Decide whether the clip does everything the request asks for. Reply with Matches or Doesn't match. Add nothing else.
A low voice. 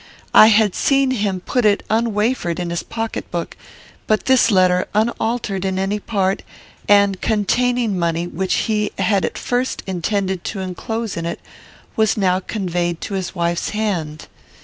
Doesn't match